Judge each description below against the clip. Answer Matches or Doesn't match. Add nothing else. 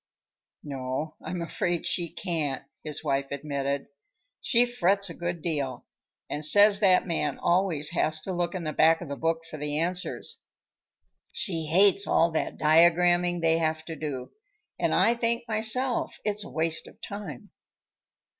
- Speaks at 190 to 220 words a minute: Doesn't match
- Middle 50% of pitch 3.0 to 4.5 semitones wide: Matches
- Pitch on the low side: Doesn't match